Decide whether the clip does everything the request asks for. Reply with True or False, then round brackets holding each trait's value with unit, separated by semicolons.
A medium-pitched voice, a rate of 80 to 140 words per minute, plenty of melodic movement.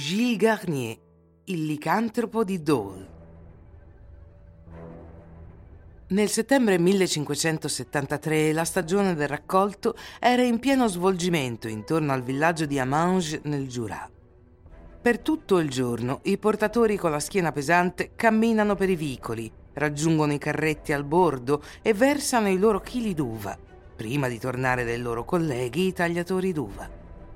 True (150 Hz; 125 wpm; 8.9 semitones)